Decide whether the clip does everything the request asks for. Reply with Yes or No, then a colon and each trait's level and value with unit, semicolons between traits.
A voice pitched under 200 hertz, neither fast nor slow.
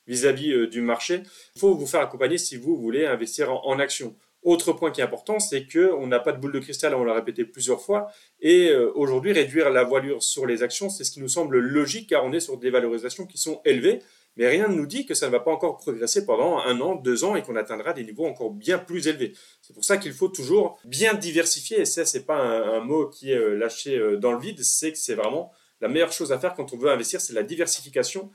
No: high, 190 Hz; fast, 250 wpm